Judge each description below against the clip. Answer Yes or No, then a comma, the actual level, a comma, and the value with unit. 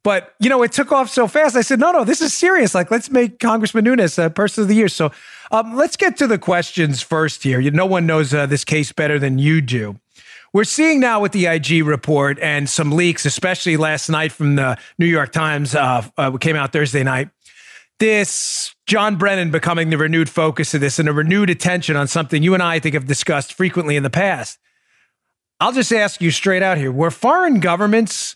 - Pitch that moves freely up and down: Yes, wide, 6.5 semitones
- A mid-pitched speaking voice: Yes, medium, 170 Hz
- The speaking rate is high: Yes, fast, 220 wpm